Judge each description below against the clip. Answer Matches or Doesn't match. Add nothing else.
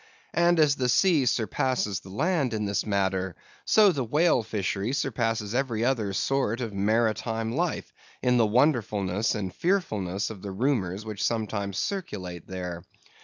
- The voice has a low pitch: Matches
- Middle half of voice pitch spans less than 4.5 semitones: Doesn't match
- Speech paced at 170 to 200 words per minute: Doesn't match